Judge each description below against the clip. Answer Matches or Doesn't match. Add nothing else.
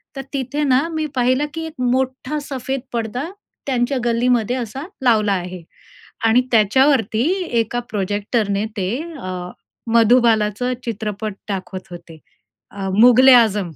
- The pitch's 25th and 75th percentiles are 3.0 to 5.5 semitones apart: Matches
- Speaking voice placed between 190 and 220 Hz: Doesn't match